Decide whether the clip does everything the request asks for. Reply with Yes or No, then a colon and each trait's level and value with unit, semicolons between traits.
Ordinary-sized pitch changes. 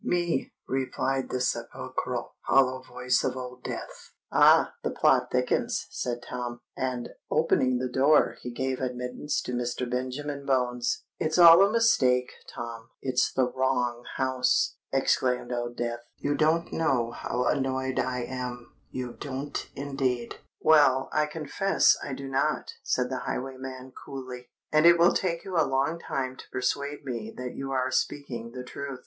No: narrow, 2.1 semitones